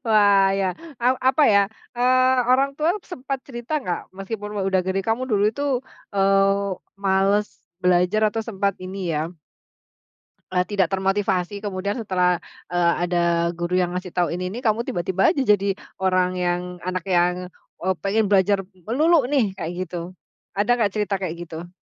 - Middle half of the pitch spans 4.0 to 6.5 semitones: No, average, 3.0 semitones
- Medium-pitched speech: No, high, 195 Hz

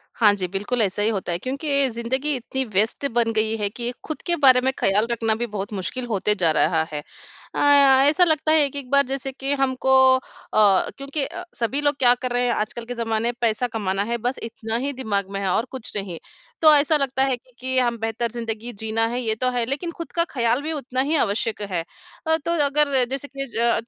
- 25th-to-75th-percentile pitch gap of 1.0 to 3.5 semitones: No, average, 3.9 semitones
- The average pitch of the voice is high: Yes, high, 240 Hz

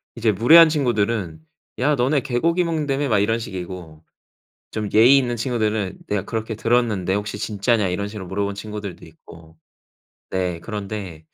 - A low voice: Yes, low, 105 Hz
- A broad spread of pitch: No, average, 4.1 semitones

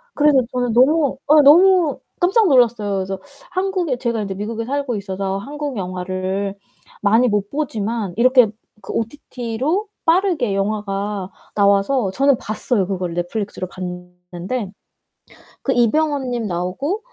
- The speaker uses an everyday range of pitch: No, wide, 6.1 semitones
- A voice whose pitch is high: Yes, high, 225 Hz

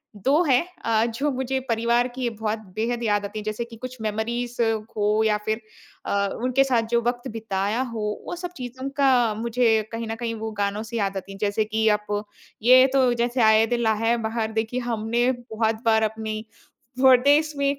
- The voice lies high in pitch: Yes, high, 230 Hz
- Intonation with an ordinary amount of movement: No, narrow, 2.3 semitones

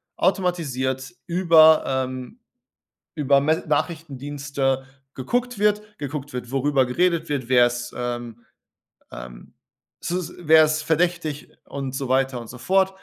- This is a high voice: No, medium, 145 Hz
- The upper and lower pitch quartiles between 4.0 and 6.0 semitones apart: Yes, average, 4.5 semitones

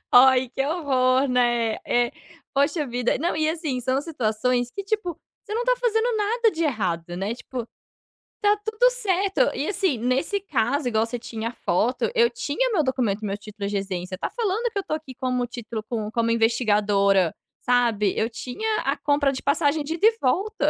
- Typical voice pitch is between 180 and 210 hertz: No, very high, 255 Hz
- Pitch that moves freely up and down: Yes, wide, 8.1 semitones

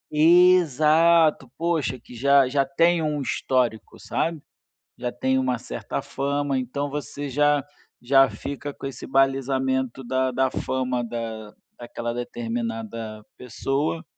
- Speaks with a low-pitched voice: Yes, low, 130 Hz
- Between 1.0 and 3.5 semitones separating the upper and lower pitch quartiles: Yes, average, 3.0 semitones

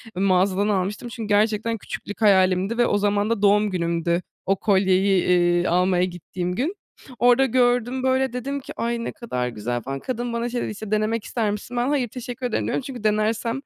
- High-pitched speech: Yes, high, 210 Hz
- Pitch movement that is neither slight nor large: Yes, average, 4.4 semitones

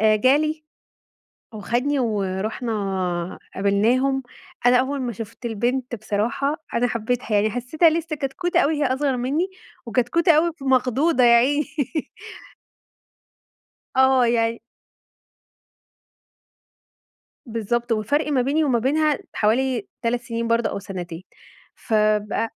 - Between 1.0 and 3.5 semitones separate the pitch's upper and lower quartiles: No, average, 4.0 semitones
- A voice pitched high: Yes, high, 245 Hz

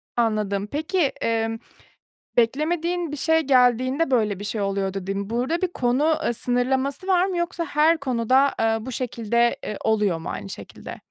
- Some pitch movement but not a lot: No, wide, 5.7 semitones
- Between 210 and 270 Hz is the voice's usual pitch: Yes, high, 245 Hz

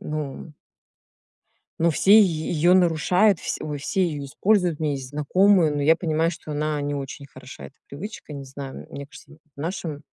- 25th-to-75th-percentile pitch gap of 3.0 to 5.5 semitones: Yes, average, 3.5 semitones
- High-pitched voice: No, medium, 155 Hz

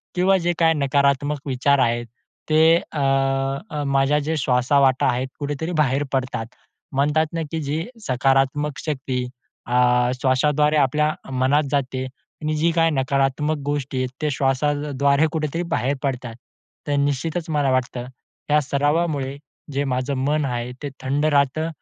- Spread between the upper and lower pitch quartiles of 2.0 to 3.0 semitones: Yes, narrow, 2.4 semitones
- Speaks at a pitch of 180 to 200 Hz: No, medium, 140 Hz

